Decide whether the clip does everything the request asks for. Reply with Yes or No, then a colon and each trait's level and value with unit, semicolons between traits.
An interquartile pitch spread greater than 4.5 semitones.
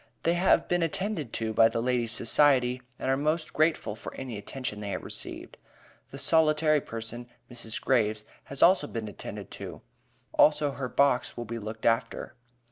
Yes: average, 5.0 semitones